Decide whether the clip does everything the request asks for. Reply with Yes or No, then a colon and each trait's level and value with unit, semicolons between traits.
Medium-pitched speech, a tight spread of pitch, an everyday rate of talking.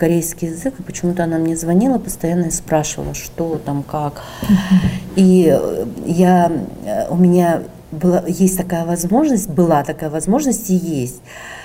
Yes: medium, 170 Hz; narrow, 2.2 semitones; average, 135 wpm